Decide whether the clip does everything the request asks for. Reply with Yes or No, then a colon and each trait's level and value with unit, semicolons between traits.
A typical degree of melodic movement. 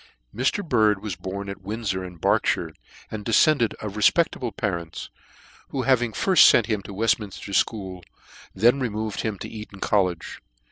Yes: average, 3.2 semitones